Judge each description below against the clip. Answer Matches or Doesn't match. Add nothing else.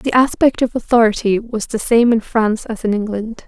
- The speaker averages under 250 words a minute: Matches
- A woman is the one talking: Matches